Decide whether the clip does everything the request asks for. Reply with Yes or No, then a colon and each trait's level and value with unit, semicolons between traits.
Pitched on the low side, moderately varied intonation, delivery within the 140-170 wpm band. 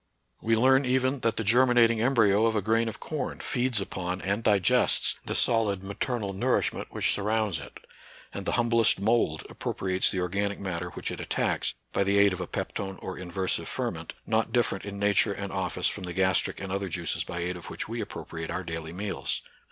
No: low, 100 Hz; average, 3.5 semitones; average, 195 wpm